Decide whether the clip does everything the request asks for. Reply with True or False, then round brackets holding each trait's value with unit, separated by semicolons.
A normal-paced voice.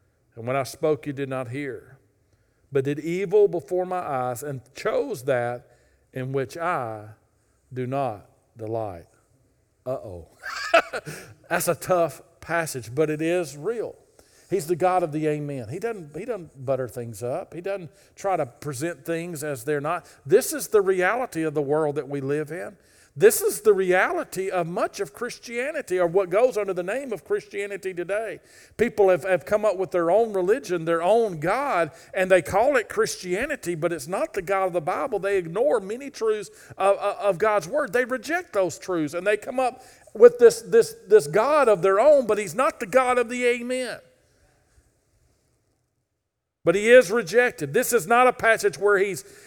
True (180 wpm)